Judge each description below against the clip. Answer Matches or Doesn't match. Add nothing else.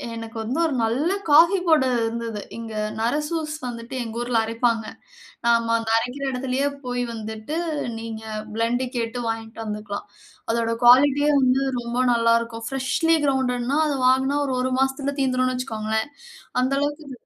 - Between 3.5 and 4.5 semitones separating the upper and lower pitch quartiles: Doesn't match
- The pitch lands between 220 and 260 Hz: Matches